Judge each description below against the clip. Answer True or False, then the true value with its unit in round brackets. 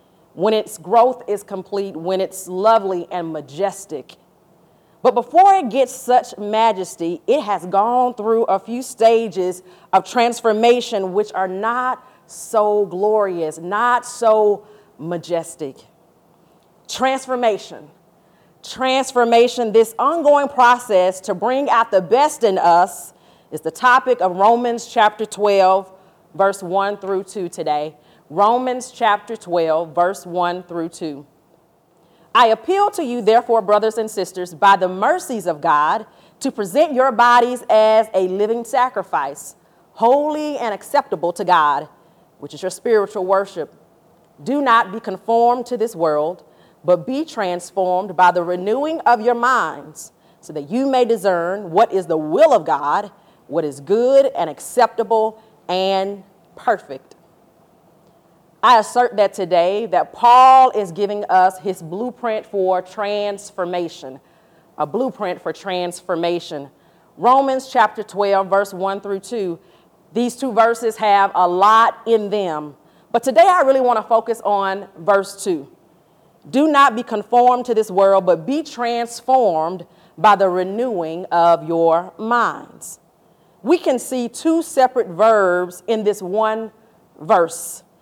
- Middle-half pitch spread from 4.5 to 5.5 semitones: True (4.9 semitones)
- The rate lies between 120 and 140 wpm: True (135 wpm)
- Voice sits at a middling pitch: False (205 Hz)